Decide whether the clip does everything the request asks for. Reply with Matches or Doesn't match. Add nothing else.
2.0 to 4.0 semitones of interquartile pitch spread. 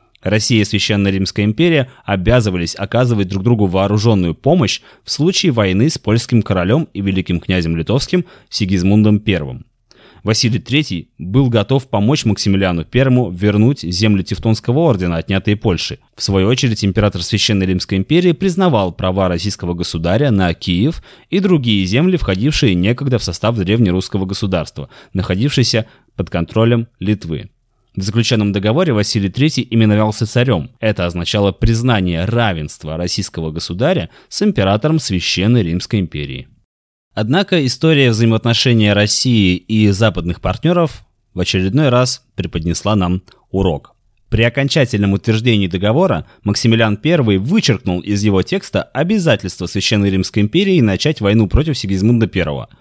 Doesn't match